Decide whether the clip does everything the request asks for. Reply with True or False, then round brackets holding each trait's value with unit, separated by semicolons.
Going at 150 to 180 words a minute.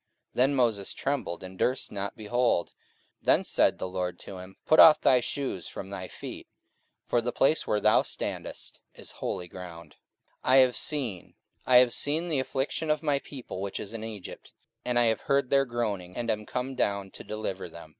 False (195 wpm)